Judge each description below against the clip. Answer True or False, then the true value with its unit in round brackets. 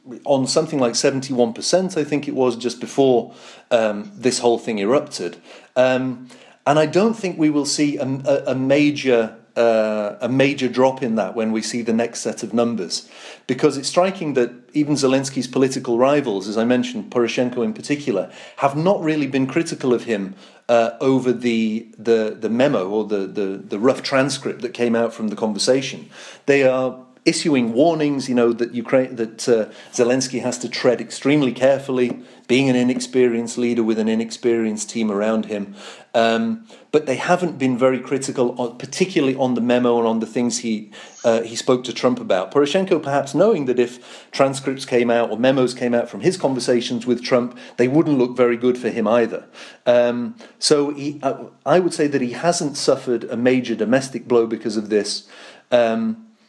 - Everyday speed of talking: True (185 wpm)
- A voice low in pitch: True (125 Hz)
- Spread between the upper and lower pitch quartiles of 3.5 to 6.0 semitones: False (2.8 semitones)